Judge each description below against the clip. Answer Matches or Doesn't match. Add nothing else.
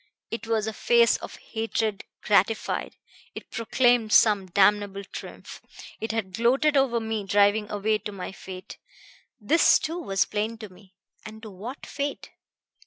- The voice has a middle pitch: Doesn't match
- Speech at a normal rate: Matches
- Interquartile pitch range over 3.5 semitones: Doesn't match